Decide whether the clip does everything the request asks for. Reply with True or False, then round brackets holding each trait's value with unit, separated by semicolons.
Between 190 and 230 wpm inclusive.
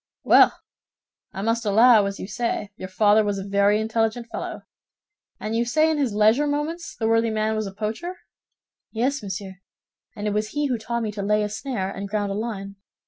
True (200 wpm)